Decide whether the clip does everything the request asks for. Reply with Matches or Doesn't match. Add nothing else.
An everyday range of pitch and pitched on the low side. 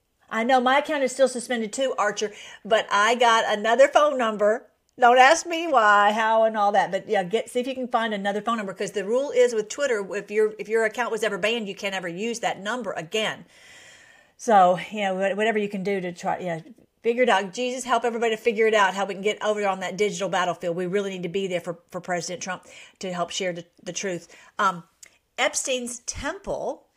Doesn't match